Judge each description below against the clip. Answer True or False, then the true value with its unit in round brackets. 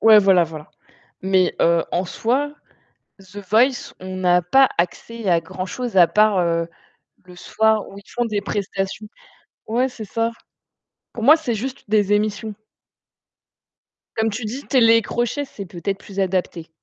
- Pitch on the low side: False (205 Hz)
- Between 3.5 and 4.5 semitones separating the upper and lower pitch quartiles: True (3.8 semitones)